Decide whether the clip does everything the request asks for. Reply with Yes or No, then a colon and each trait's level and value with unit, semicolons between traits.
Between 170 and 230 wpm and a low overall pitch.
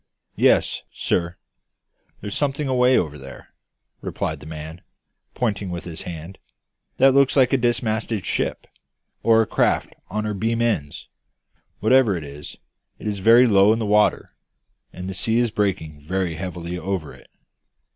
No: average, 155 wpm; low, 100 Hz